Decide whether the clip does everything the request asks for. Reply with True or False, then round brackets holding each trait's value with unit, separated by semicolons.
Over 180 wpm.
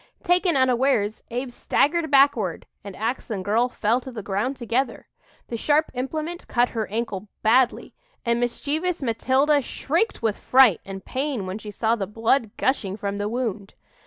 False (160 wpm)